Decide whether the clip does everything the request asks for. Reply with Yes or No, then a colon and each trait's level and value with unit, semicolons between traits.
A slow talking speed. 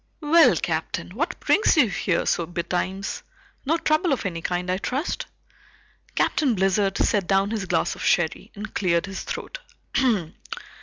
No: average, 150 wpm